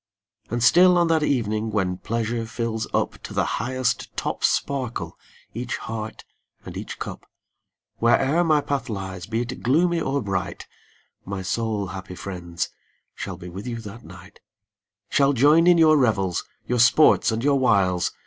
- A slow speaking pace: No, average, 160 wpm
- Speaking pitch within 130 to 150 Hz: No, low, 115 Hz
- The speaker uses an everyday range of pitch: No, wide, 5.8 semitones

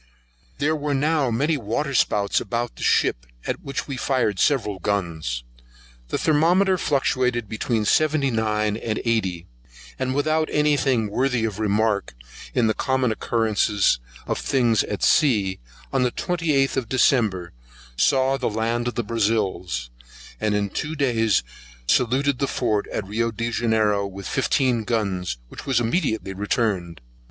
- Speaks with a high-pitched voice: No, low, 115 Hz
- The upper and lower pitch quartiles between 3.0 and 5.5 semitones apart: Yes, average, 4.6 semitones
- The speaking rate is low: No, average, 145 wpm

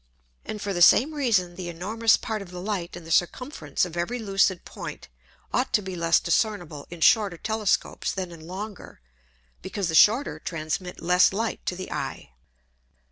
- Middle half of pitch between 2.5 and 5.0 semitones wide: Yes, average, 3.8 semitones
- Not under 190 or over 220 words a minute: No, average, 175 wpm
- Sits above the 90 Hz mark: Yes, medium, 185 Hz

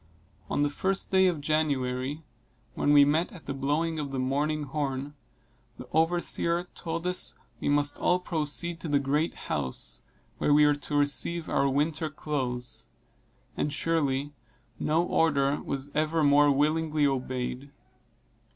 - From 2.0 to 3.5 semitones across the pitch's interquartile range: Yes, narrow, 2.6 semitones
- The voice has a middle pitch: Yes, medium, 145 Hz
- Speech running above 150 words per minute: No, average, 145 wpm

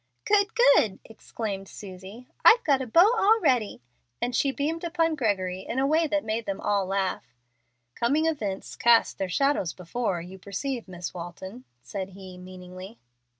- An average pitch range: No, wide, 7.2 semitones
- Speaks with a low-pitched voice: No, high, 220 Hz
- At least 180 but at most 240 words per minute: No, average, 155 wpm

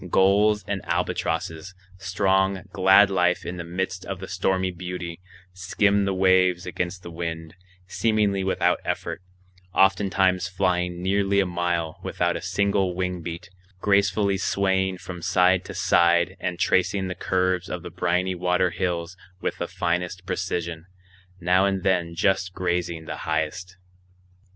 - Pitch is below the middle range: Yes, very low, 90 Hz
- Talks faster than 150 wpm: No, average, 140 wpm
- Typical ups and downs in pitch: No, narrow, 1.5 semitones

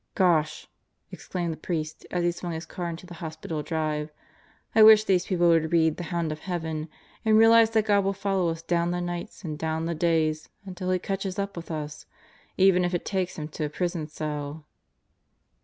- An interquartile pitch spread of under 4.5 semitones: Yes, average, 2.8 semitones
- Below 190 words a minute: No, average, 200 wpm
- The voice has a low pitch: No, medium, 170 Hz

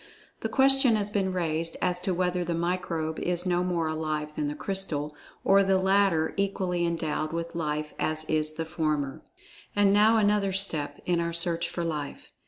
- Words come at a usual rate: Yes, average, 180 wpm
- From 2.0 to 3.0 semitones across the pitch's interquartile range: No, average, 3.5 semitones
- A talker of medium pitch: Yes, medium, 170 Hz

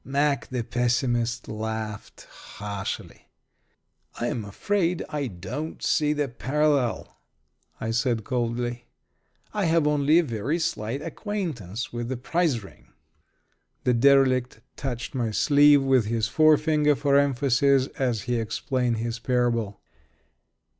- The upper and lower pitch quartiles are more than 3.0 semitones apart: Yes, average, 4.0 semitones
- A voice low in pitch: Yes, low, 125 Hz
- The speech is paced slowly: Yes, slow, 120 wpm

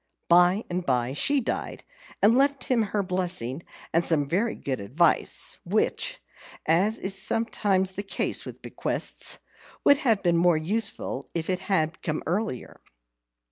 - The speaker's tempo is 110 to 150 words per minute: Yes, average, 145 wpm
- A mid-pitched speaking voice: Yes, medium, 180 Hz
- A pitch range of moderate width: Yes, average, 4.6 semitones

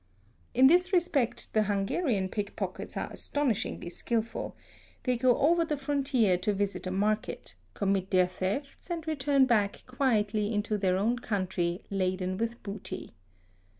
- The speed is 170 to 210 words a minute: No, average, 140 wpm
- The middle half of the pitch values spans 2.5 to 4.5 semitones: No, wide, 5.5 semitones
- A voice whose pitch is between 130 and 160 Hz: No, high, 215 Hz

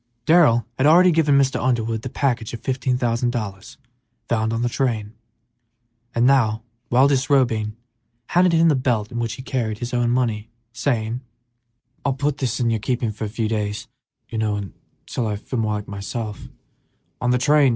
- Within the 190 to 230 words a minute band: No, average, 160 wpm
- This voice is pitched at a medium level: No, low, 120 Hz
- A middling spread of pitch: Yes, average, 3.1 semitones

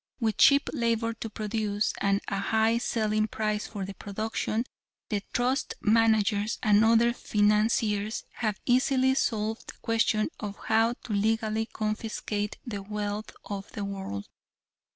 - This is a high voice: Yes, high, 215 Hz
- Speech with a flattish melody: Yes, narrow, 1.6 semitones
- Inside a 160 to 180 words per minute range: No, slow, 135 wpm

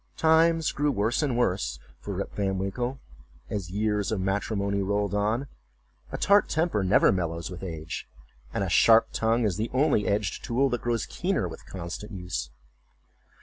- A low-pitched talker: Yes, low, 105 Hz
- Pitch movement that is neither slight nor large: Yes, average, 4.1 semitones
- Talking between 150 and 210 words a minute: Yes, average, 165 wpm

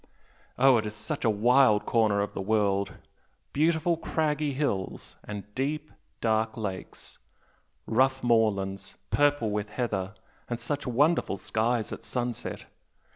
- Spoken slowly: Yes, slow, 130 wpm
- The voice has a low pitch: Yes, low, 115 Hz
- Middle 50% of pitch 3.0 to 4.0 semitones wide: No, average, 4.7 semitones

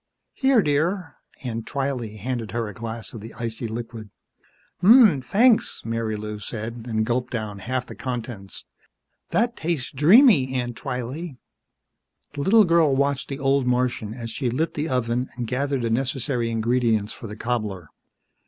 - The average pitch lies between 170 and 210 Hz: No, low, 125 Hz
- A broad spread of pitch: No, average, 3.7 semitones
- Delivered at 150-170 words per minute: Yes, average, 155 wpm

